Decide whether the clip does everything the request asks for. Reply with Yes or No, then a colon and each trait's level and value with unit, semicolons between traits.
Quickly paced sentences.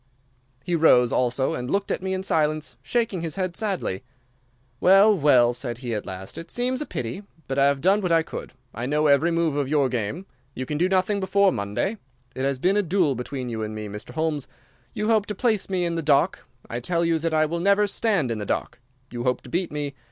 Yes: fast, 235 wpm